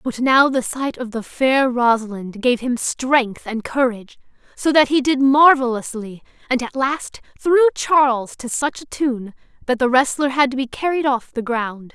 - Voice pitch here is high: Yes, very high, 255 Hz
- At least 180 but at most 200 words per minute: Yes, average, 185 wpm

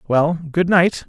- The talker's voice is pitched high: No, medium, 165 Hz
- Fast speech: No, average, 165 wpm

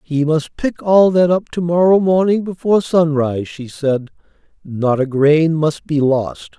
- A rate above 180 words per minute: No, average, 175 wpm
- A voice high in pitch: No, medium, 160 Hz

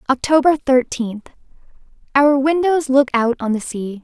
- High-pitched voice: Yes, very high, 265 Hz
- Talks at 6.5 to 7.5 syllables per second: No, 4.4 syllables/s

